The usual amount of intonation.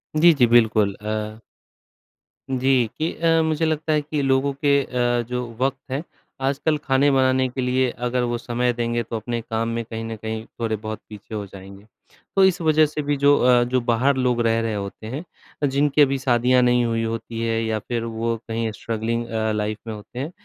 Yes: average, 3.2 semitones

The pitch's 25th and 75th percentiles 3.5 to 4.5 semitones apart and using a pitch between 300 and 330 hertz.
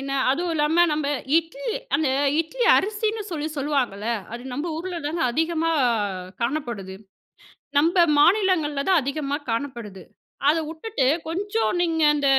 Yes: average, 4.0 semitones; very high, 310 Hz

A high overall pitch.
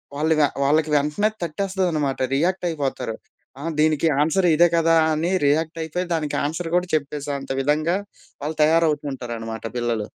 No: medium, 155 Hz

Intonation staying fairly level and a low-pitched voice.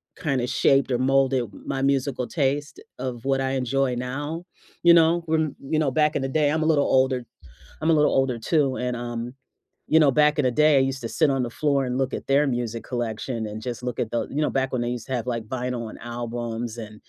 No: average, 3.0 semitones; low, 130 Hz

